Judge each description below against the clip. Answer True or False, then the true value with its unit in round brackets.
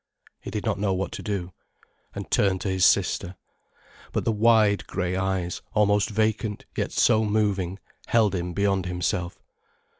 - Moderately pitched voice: False (100 Hz)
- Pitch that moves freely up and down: False (2.5 semitones)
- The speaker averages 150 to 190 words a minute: True (155 wpm)